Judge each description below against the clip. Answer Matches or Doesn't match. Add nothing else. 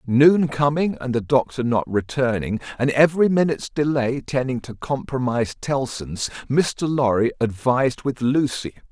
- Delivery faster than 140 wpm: Doesn't match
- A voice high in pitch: Doesn't match